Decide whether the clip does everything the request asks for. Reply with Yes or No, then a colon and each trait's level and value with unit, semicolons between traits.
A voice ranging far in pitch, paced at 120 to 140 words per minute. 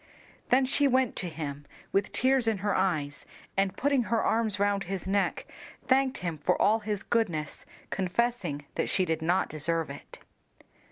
No: wide, 5.9 semitones; average, 165 wpm